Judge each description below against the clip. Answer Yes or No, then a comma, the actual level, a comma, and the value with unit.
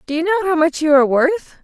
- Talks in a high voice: Yes, very high, 325 Hz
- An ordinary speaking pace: No, fast, 295 wpm